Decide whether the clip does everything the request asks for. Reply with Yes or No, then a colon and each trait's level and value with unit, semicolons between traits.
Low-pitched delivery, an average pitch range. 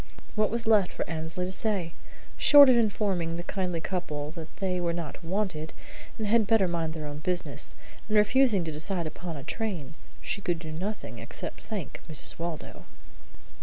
No: medium, 180 Hz; average, 4.4 semitones